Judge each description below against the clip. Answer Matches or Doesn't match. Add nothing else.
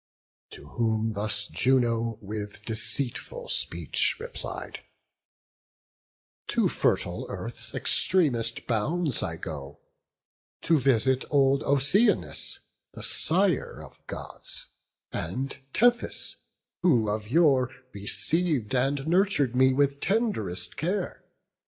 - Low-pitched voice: Matches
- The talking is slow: Matches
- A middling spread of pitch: Doesn't match